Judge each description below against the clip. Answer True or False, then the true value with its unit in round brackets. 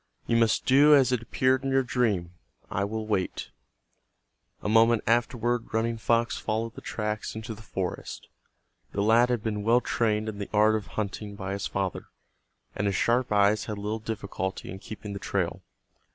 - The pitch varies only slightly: True (2.3 semitones)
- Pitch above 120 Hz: False (110 Hz)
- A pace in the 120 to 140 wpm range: False (180 wpm)